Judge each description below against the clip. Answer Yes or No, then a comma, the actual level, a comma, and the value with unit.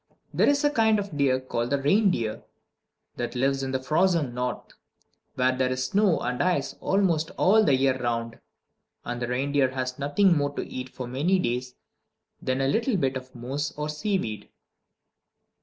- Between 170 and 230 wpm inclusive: Yes, average, 175 wpm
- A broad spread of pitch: Yes, wide, 5.7 semitones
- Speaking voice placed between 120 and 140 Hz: Yes, low, 135 Hz